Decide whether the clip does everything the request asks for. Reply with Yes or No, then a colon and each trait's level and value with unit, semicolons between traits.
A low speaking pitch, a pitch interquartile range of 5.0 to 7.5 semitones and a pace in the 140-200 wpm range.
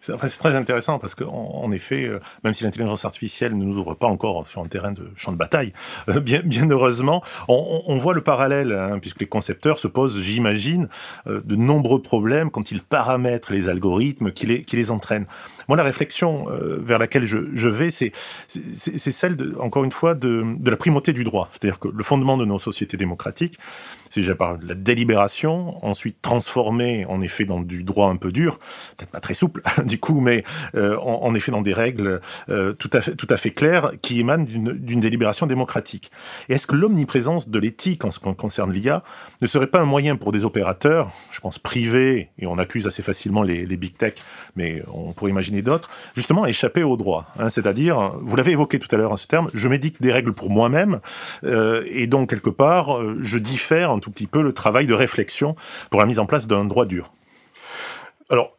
No: low, 120 Hz; wide, 5.5 semitones; average, 210 wpm